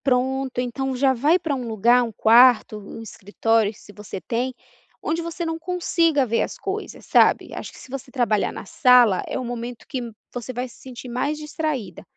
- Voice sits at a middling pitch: No, very high, 250 Hz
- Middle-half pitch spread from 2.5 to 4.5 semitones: Yes, average, 3.6 semitones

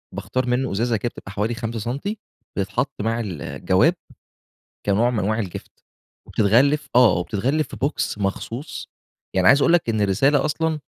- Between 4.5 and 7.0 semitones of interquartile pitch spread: Yes, average, 5.0 semitones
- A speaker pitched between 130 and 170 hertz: No, low, 120 Hz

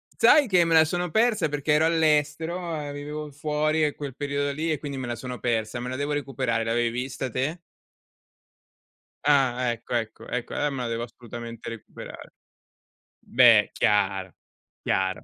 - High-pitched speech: No, medium, 140 Hz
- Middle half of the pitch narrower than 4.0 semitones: No, average, 4.3 semitones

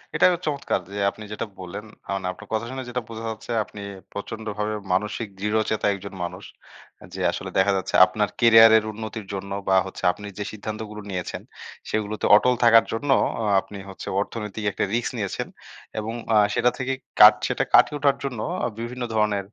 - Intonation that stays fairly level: Yes, narrow, 2.2 semitones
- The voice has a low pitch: Yes, low, 110 Hz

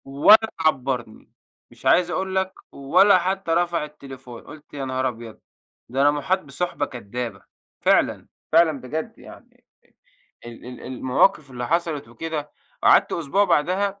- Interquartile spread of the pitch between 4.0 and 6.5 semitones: Yes, average, 5.2 semitones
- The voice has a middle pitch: Yes, medium, 150 Hz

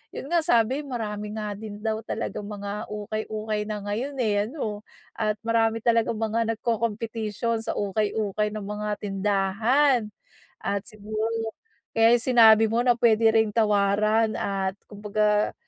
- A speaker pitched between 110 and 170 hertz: No, high, 215 Hz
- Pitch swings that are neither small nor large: No, narrow, 1.5 semitones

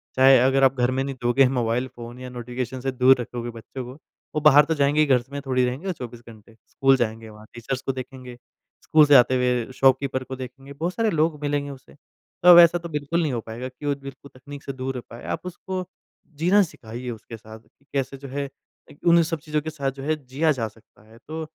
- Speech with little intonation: No, average, 3.0 semitones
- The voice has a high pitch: No, low, 135 Hz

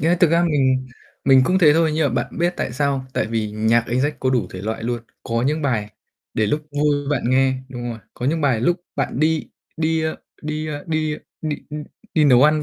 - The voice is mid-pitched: Yes, medium, 145 Hz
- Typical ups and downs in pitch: Yes, average, 4.2 semitones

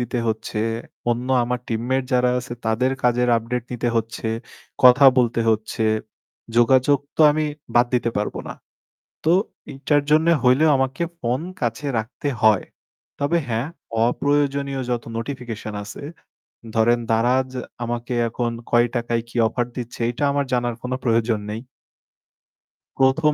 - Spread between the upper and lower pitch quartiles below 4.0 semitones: Yes, narrow, 2.4 semitones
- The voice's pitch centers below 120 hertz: No, low, 125 Hz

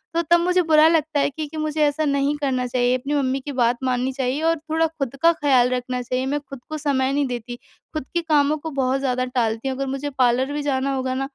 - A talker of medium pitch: No, very high, 275 Hz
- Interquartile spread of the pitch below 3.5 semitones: Yes, average, 3.0 semitones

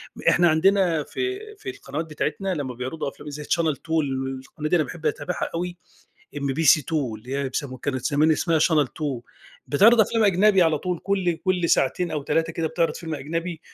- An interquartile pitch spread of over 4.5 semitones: No, average, 3.8 semitones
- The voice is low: No, medium, 160 Hz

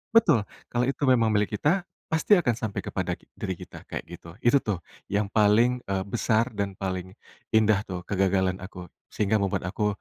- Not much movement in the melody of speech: No, average, 3.9 semitones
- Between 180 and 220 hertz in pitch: No, low, 105 Hz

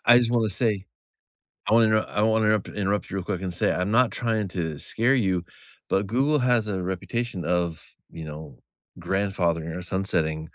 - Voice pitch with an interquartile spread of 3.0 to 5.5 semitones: Yes, average, 4.1 semitones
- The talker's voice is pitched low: Yes, low, 100 Hz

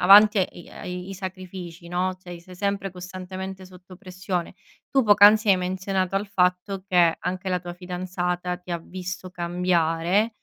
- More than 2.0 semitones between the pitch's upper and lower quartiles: No, narrow, 1.4 semitones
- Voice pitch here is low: No, medium, 185 Hz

